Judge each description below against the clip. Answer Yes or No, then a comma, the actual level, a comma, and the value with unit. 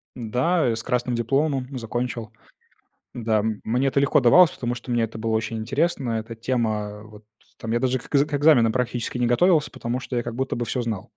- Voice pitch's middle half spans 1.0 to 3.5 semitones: Yes, narrow, 2.5 semitones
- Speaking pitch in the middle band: No, low, 120 Hz